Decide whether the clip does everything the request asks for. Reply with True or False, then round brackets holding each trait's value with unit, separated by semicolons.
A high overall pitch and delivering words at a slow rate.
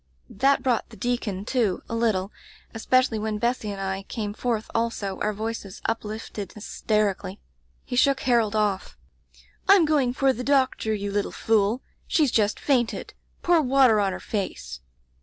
False (220 Hz; 160 wpm)